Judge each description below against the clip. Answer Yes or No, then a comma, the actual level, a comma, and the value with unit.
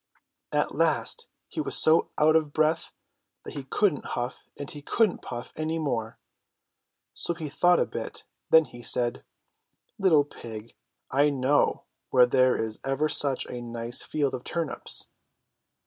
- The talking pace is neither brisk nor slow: Yes, average, 150 wpm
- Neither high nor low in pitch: Yes, medium, 145 Hz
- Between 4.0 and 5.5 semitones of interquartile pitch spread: Yes, average, 4.3 semitones